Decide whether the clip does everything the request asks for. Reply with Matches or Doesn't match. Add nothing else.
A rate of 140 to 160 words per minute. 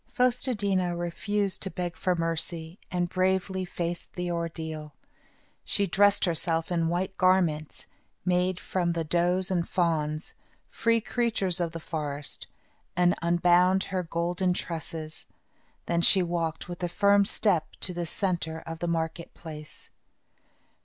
Matches